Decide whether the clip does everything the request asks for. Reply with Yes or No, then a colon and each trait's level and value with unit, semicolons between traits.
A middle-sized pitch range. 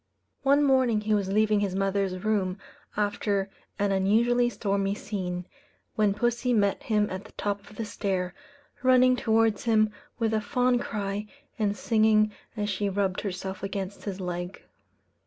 No: narrow, 2.1 semitones